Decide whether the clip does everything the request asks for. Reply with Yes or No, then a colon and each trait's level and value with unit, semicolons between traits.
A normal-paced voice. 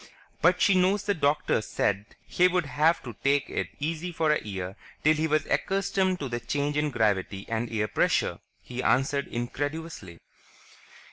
Yes: average, 160 wpm